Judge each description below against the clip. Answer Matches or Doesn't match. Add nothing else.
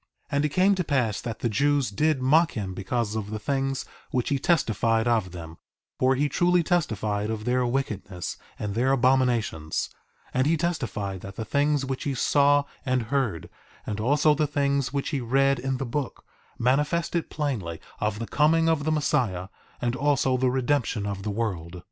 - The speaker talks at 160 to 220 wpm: Matches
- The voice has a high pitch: Doesn't match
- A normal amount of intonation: Matches